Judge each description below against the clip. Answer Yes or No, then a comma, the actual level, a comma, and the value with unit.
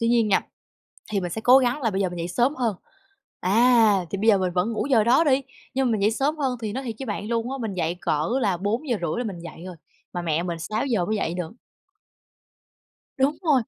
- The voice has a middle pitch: No, high, 220 Hz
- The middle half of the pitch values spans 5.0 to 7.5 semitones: Yes, average, 5.3 semitones